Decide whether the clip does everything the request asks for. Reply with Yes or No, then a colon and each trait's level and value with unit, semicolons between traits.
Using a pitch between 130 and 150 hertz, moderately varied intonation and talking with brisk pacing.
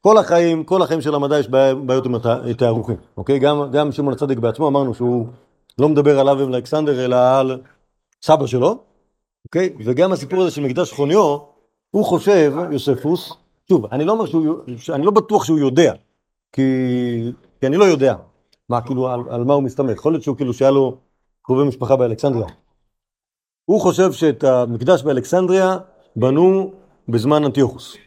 Yes: medium, 140 Hz; average, 4.3 semitones; fast, 160 wpm